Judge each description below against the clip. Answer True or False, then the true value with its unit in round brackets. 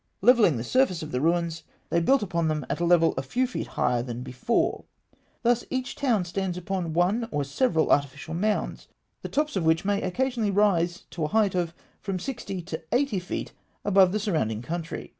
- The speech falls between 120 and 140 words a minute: False (195 wpm)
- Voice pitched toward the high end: False (180 Hz)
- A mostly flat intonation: False (4.9 semitones)